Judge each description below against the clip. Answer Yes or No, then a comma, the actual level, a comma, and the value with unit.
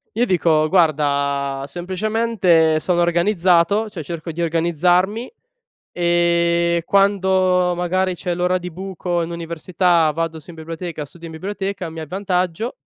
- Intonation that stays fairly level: Yes, narrow, 2.2 semitones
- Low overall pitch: No, medium, 175 Hz